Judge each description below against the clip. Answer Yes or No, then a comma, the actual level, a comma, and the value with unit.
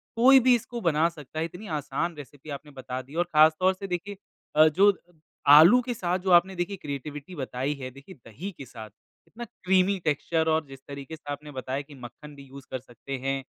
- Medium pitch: Yes, medium, 155 Hz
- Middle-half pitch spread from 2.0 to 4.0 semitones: No, average, 5.1 semitones